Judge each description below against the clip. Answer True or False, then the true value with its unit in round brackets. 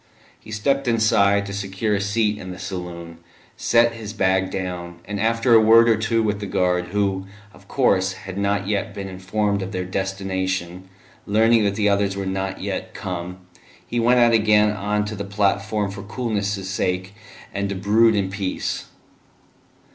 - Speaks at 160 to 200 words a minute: True (175 wpm)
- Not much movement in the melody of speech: True (2.2 semitones)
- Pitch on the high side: False (100 Hz)